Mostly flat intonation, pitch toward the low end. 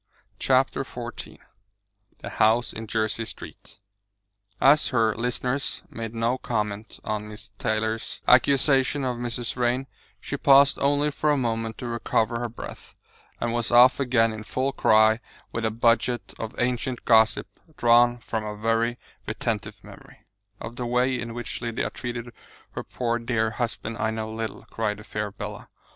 Yes: narrow, 1.8 semitones; low, 115 Hz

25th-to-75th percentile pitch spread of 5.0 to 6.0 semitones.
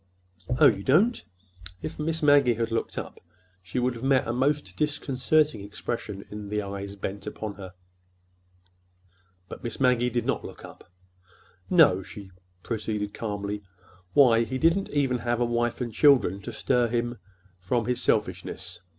No: average, 4.4 semitones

